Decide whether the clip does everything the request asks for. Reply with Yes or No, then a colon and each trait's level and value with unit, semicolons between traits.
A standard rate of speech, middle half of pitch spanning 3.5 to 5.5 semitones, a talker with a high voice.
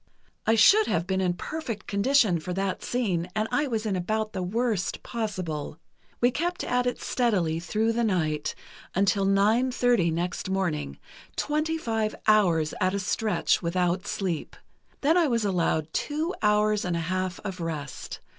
Yes: average, 165 wpm; average, 4.6 semitones; high, 200 Hz